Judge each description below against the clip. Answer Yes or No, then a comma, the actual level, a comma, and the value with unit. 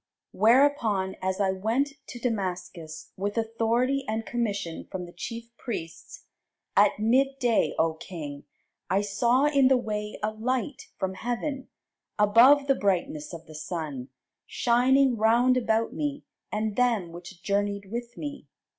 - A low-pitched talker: No, high, 220 Hz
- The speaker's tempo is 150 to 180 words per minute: No, slow, 135 wpm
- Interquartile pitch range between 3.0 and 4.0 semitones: No, average, 4.8 semitones